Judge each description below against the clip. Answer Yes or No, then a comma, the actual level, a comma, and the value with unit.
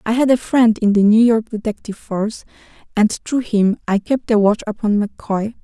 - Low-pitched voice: No, high, 220 Hz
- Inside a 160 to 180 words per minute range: No, average, 200 wpm